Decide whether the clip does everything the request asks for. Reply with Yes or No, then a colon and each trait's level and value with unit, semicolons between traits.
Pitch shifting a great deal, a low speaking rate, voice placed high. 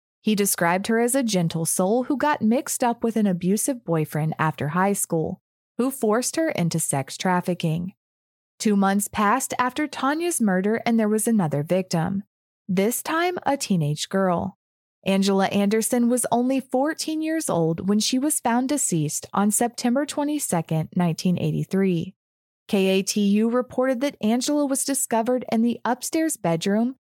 No: wide, 5.7 semitones; average, 145 wpm; high, 215 Hz